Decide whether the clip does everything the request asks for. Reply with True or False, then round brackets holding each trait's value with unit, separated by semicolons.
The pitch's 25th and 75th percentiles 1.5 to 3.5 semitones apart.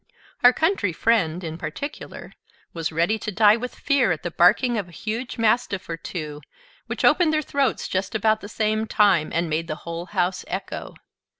False (5.4 semitones)